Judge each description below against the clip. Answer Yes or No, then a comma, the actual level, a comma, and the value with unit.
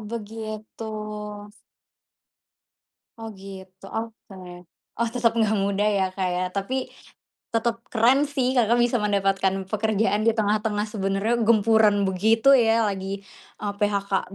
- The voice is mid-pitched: No, high, 215 Hz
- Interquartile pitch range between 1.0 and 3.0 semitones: Yes, narrow, 2.5 semitones